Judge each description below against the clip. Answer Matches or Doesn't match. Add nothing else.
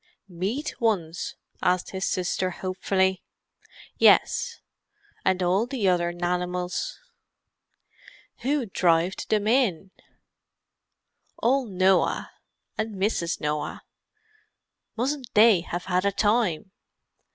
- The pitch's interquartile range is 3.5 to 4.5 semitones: Matches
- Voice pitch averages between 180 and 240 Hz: Matches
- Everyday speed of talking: Doesn't match